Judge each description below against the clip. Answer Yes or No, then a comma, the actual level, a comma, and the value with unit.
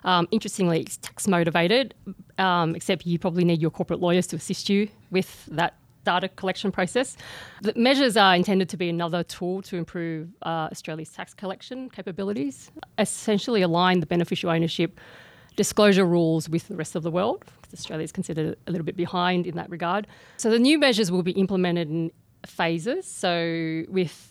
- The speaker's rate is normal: Yes, average, 175 wpm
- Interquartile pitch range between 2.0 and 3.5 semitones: Yes, average, 2.7 semitones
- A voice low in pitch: No, medium, 180 Hz